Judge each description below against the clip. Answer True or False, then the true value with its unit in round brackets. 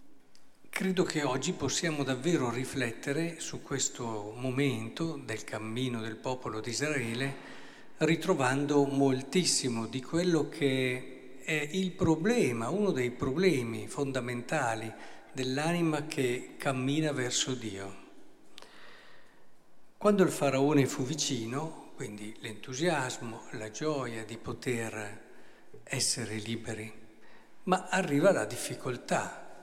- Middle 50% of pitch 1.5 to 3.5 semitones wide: False (4.7 semitones)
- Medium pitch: False (130 Hz)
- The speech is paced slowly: True (100 wpm)